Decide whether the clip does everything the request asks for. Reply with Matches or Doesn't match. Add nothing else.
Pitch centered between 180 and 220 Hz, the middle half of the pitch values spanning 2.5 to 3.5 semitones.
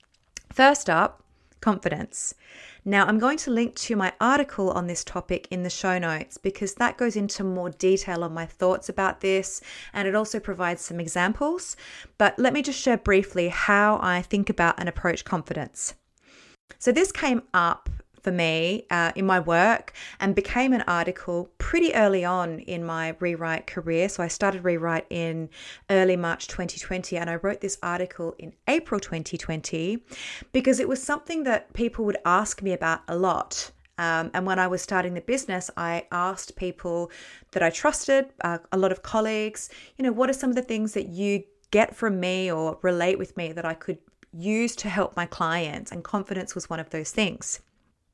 Doesn't match